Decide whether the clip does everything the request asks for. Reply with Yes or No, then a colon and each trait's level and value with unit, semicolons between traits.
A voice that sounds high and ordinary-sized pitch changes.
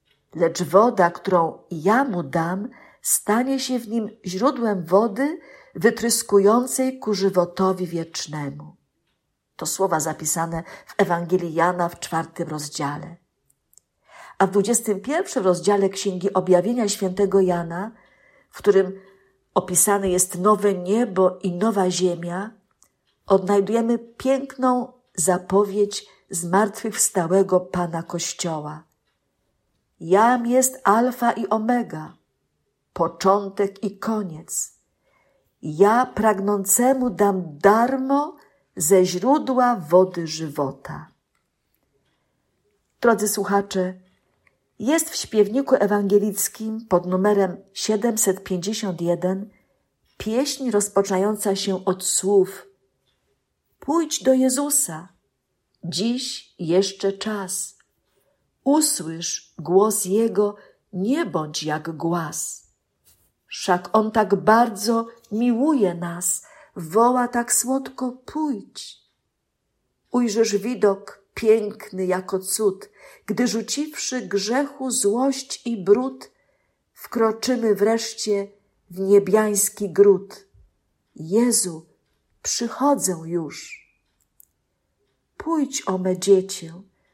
Yes: high, 200 Hz; average, 4.2 semitones